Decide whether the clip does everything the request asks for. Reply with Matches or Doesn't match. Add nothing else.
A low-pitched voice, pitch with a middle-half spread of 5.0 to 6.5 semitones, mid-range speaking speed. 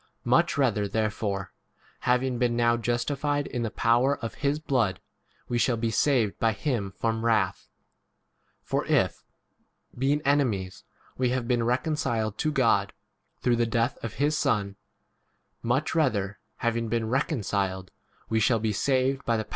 Doesn't match